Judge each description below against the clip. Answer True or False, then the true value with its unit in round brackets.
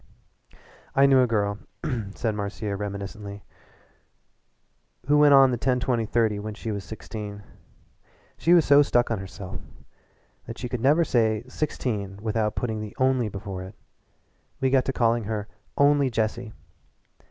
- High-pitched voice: False (115 Hz)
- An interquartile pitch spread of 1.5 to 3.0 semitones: False (3.9 semitones)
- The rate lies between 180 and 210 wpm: False (150 wpm)